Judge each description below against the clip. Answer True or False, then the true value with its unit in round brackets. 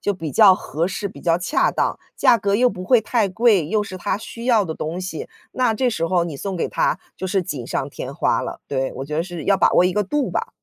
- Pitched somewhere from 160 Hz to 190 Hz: True (185 Hz)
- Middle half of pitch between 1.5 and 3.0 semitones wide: False (4.5 semitones)